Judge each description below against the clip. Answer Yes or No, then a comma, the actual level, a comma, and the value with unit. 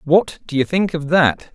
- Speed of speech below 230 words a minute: No, fast, 235 wpm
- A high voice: No, medium, 160 Hz